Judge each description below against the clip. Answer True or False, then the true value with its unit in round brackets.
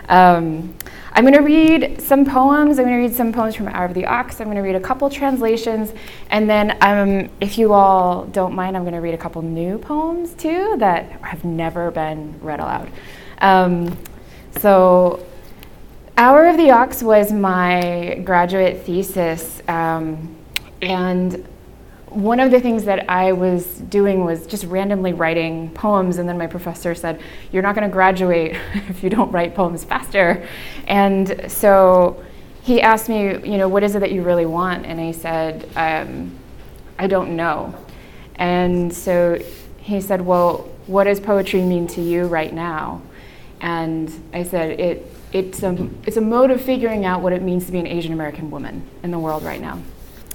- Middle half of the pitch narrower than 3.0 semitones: False (3.4 semitones)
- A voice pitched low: False (185 Hz)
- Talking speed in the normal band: True (180 wpm)